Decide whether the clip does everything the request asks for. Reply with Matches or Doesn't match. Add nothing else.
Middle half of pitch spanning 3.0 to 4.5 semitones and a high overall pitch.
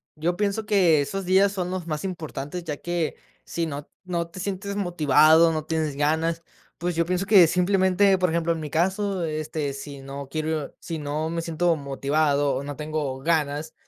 Doesn't match